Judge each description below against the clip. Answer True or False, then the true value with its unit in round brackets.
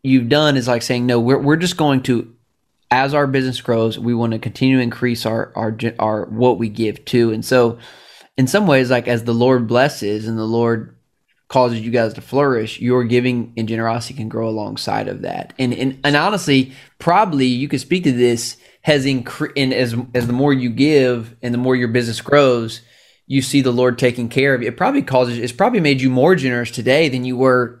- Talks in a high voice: False (125 Hz)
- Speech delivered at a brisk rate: True (220 wpm)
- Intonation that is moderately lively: False (2.3 semitones)